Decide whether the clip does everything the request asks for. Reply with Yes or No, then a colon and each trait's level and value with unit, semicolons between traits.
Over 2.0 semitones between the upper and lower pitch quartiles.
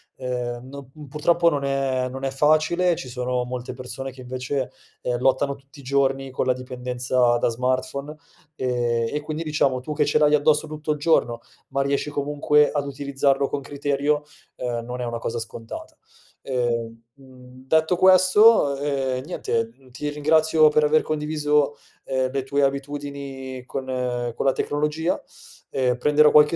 Yes: average, 2.7 semitones